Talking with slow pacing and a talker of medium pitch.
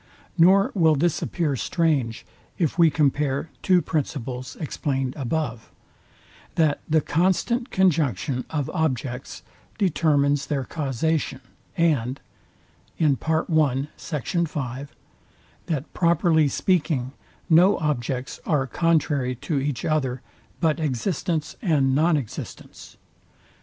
Yes: slow, 95 wpm; medium, 150 Hz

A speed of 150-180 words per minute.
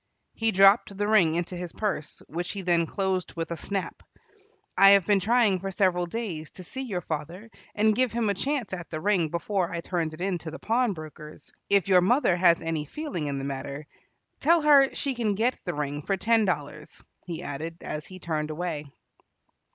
No: average, 200 wpm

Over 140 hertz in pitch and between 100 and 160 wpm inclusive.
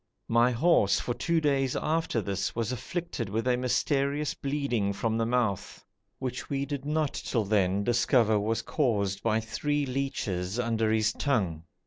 No: low, 120 Hz; average, 155 wpm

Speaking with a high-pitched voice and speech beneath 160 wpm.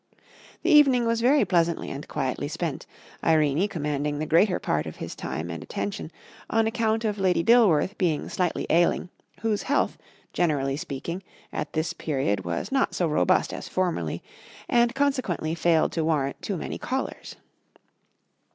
No: medium, 170 Hz; average, 150 wpm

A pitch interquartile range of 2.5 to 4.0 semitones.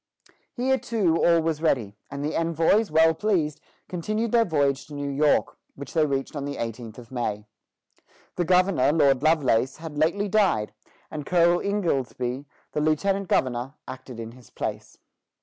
No: average, 4.8 semitones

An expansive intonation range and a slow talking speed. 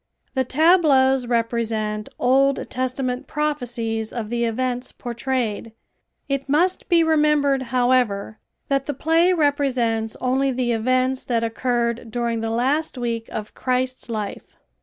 No: average, 2.9 semitones; slow, 125 wpm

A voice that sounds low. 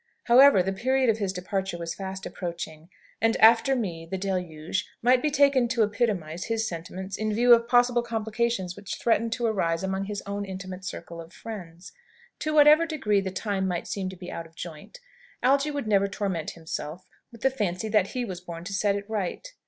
No: high, 200 Hz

